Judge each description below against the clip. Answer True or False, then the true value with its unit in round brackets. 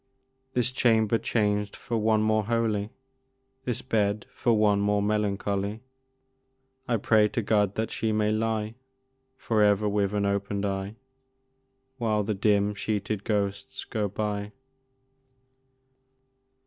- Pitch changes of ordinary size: False (1.4 semitones)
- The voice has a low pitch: True (105 Hz)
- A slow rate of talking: True (120 wpm)